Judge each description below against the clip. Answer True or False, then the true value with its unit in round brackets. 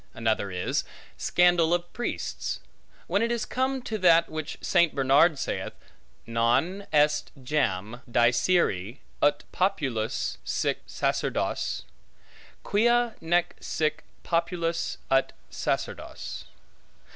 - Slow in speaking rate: True (100 wpm)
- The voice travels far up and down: True (6.2 semitones)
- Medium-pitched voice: True (160 Hz)